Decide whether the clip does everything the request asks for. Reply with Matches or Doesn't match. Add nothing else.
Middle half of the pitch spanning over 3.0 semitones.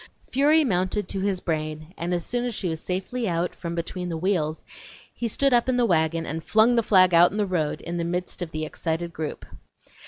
Matches